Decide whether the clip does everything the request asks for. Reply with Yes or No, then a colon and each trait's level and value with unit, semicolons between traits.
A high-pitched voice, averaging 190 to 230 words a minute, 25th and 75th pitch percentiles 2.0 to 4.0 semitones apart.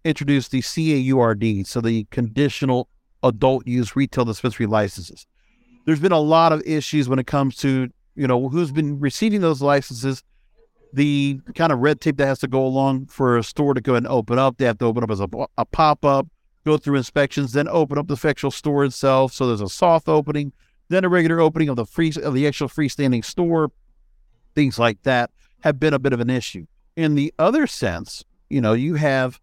No: medium, 140 Hz; fast, 205 wpm; average, 3.2 semitones